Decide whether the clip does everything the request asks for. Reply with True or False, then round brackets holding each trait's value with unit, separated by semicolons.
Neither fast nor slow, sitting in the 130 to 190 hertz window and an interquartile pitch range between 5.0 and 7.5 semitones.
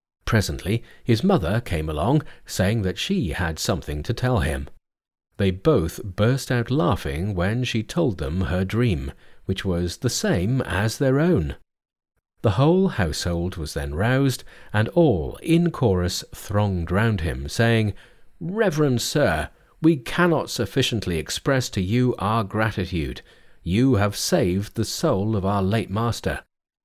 False (145 wpm; 105 Hz; 5.3 semitones)